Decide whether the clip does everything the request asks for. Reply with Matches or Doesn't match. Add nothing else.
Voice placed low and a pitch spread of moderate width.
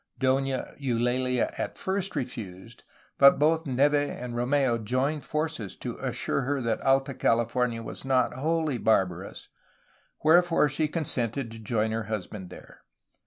Matches